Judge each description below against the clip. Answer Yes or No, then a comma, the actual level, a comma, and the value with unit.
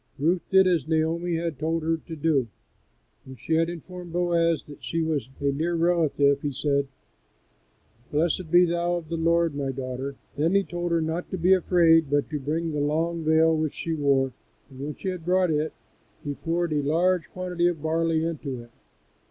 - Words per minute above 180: Yes, average, 195 wpm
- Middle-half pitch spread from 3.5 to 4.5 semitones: No, average, 2.7 semitones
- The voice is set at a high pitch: No, medium, 160 Hz